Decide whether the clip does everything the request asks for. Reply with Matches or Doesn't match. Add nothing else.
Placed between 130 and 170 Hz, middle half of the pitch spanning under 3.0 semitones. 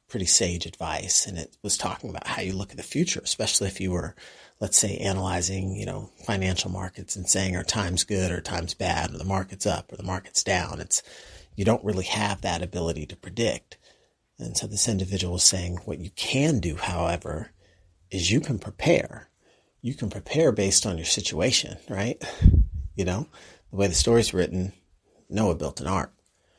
Doesn't match